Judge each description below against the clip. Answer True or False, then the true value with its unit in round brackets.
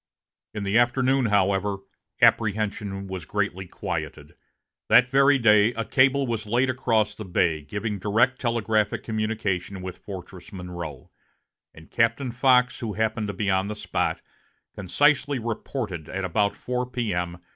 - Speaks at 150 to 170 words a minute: False (140 wpm)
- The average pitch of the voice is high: False (105 Hz)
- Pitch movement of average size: True (4.0 semitones)